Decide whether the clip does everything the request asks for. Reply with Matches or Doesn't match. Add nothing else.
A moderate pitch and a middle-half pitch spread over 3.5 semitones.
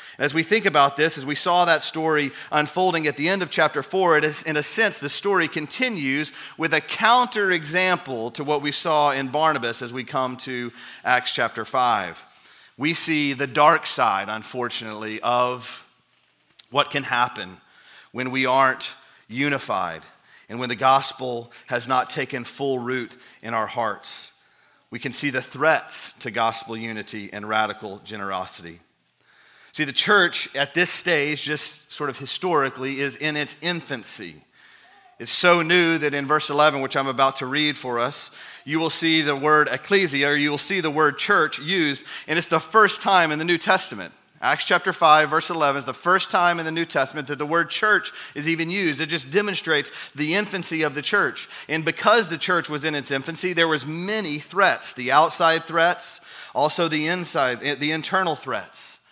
Matches